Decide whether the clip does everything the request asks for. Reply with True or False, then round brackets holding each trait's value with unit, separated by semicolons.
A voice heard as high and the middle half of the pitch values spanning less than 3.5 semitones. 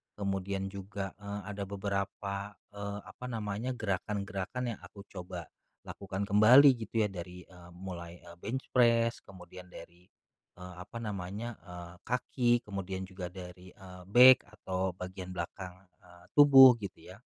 False (100 Hz; 2.6 semitones)